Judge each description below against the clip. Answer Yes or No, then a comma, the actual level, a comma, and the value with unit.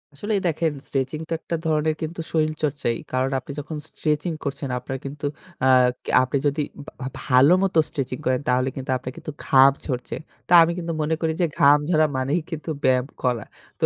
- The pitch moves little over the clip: No, average, 3.4 semitones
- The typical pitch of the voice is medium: Yes, medium, 145 Hz